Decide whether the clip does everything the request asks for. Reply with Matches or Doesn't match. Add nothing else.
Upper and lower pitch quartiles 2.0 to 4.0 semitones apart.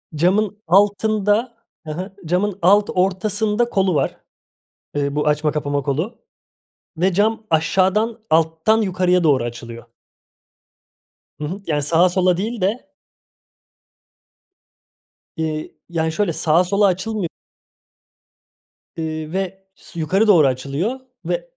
Doesn't match